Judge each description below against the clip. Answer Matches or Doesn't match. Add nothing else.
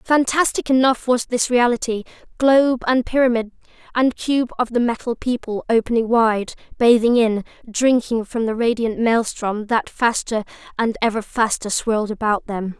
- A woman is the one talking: Matches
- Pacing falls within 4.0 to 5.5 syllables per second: Matches